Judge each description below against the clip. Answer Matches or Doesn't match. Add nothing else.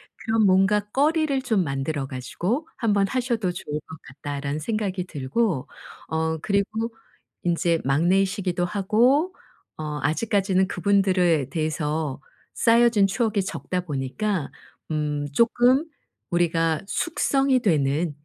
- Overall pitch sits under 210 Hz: Matches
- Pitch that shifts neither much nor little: Doesn't match